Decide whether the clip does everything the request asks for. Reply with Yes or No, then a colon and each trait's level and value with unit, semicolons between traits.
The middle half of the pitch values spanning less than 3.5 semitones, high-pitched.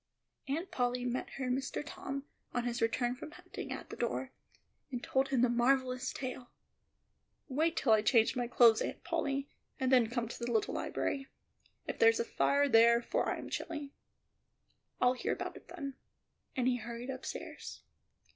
Yes: narrow, 2.4 semitones; very high, 255 Hz